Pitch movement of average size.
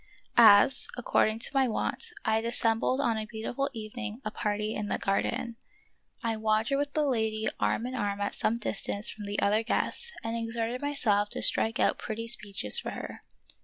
No: narrow, 2.1 semitones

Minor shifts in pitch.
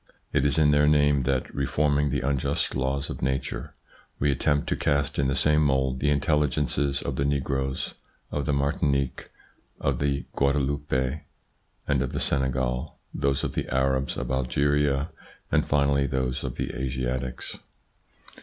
Yes: narrow, 1.4 semitones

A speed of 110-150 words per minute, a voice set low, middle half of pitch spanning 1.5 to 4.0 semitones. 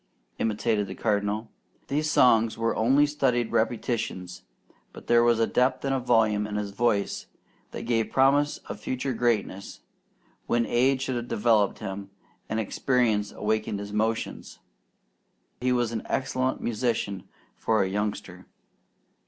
Yes: slow, 135 wpm; low, 115 Hz; average, 3.2 semitones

